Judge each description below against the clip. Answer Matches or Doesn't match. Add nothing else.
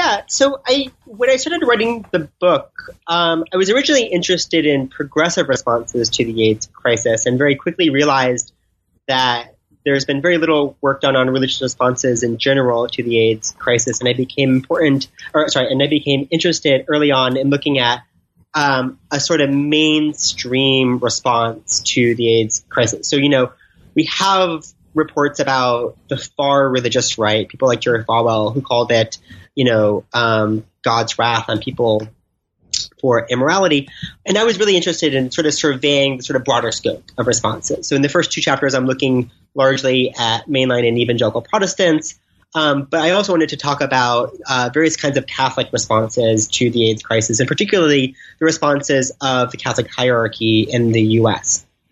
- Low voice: Matches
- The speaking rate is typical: Matches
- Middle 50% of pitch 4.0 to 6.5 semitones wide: Matches